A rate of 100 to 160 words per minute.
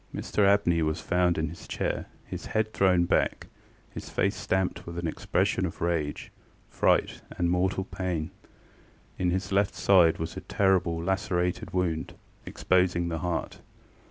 Yes: average, 155 wpm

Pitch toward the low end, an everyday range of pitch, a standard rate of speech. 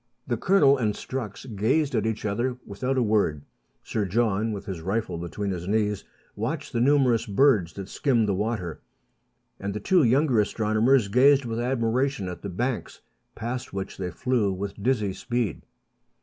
Yes: low, 110 Hz; average, 4.2 semitones; average, 165 wpm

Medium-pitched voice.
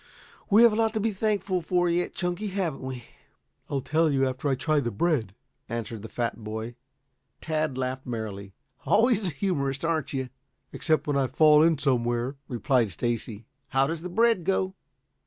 Yes: medium, 145 Hz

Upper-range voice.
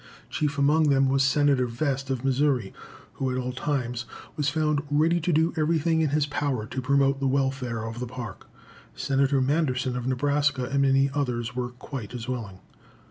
No: low, 135 Hz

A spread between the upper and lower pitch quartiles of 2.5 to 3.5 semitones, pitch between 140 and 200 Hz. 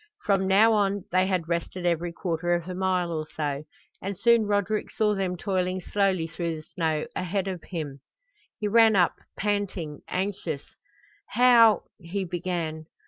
Yes: average, 3.1 semitones; medium, 185 Hz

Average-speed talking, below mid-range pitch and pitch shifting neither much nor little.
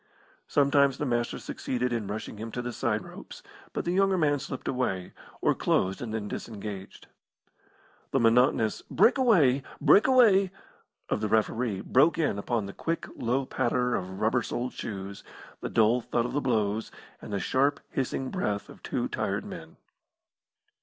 Yes: average, 165 wpm; low, 120 Hz; average, 4.6 semitones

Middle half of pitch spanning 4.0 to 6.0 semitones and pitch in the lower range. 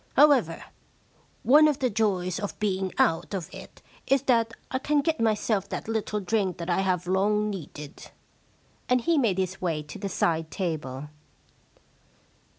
No: average, 4.5 semitones; high, 200 Hz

